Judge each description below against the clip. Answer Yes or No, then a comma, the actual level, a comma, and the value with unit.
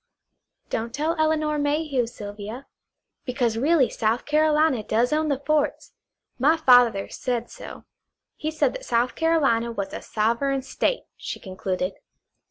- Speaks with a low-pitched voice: No, very high, 260 Hz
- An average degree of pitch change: Yes, average, 4.9 semitones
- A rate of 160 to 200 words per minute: No, slow, 135 wpm